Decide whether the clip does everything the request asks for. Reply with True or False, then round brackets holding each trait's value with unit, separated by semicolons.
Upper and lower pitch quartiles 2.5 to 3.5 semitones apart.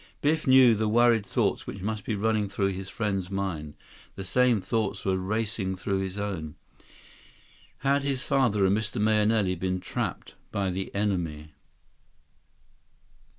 True (2.9 semitones)